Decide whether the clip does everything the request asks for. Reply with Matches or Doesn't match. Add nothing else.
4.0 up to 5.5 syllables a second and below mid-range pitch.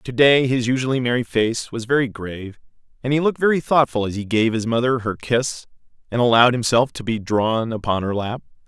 Doesn't match